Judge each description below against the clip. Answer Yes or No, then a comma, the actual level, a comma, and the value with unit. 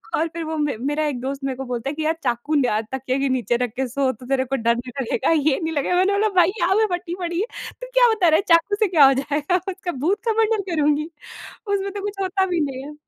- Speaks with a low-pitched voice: No, very high, 305 Hz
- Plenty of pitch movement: Yes, wide, 5.8 semitones